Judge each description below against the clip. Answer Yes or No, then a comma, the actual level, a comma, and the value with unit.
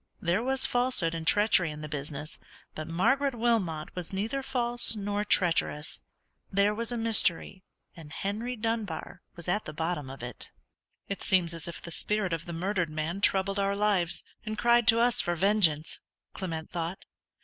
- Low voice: No, high, 190 Hz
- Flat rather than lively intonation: No, average, 4.9 semitones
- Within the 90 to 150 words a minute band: No, average, 170 wpm